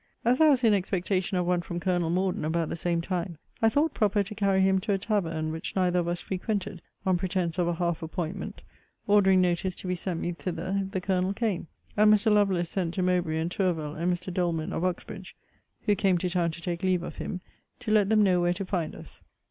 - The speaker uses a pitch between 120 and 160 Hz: No, medium, 185 Hz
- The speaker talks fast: Yes, fast, 230 wpm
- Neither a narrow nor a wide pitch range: No, narrow, 2.3 semitones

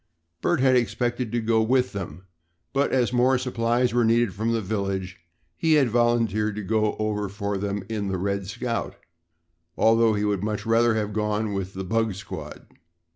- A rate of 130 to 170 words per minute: No, average, 180 wpm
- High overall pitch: No, low, 110 Hz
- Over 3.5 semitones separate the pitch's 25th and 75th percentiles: No, average, 2.8 semitones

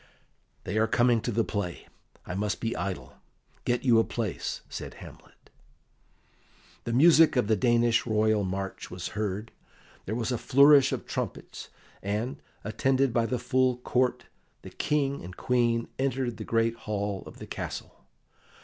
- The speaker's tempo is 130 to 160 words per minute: Yes, average, 155 wpm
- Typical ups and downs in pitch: Yes, average, 3.1 semitones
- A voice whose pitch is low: Yes, low, 115 Hz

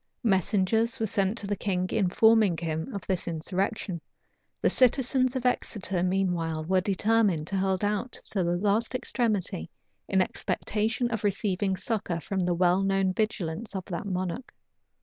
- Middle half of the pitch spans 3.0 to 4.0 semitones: Yes, average, 3.4 semitones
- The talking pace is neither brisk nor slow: Yes, average, 150 wpm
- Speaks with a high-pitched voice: Yes, high, 195 Hz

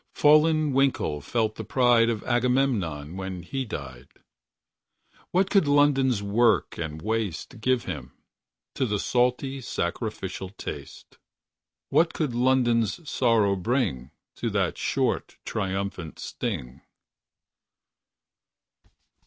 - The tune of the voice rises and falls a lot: Yes, wide, 5.8 semitones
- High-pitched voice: No, low, 115 Hz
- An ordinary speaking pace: No, slow, 105 wpm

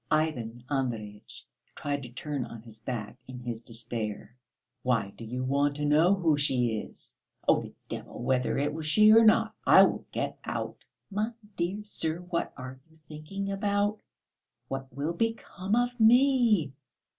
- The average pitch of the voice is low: No, medium, 145 Hz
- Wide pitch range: Yes, wide, 8.3 semitones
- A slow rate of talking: No, average, 160 wpm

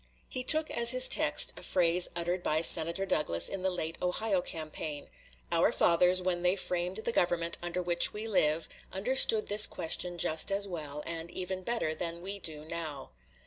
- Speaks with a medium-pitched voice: Yes, medium, 175 Hz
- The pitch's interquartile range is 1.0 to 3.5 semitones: Yes, average, 2.8 semitones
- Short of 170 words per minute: No, average, 180 wpm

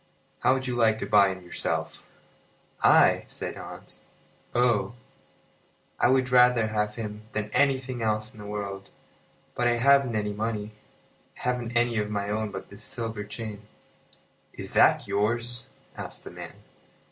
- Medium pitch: No, low, 110 Hz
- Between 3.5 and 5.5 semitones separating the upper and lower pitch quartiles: No, narrow, 2.6 semitones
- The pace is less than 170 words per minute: Yes, average, 155 wpm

